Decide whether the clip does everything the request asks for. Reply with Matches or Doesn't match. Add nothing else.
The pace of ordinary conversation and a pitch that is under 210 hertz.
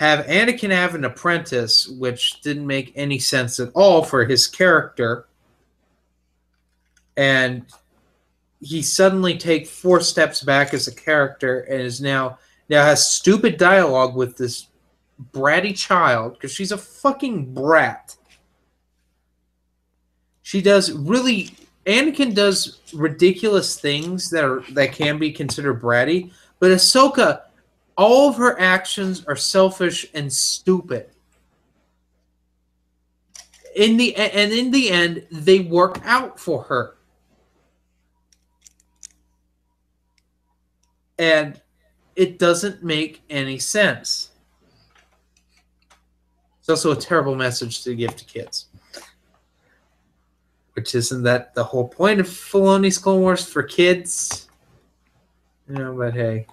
Doesn't match